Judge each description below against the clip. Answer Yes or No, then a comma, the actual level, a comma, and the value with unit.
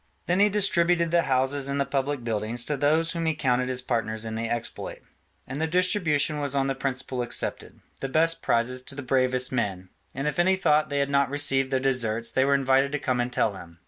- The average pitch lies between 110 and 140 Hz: Yes, low, 135 Hz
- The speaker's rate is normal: No, fast, 225 wpm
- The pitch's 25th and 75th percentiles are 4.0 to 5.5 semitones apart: No, average, 3.1 semitones